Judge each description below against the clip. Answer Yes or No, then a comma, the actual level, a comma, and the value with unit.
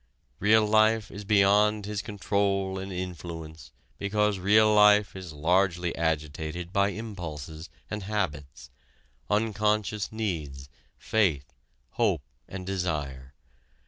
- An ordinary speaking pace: No, slow, 105 wpm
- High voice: No, very low, 95 Hz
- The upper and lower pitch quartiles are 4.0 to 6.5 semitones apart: Yes, average, 4.5 semitones